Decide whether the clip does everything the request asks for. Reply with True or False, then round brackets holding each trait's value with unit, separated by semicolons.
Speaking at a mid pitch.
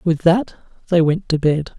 True (165 Hz)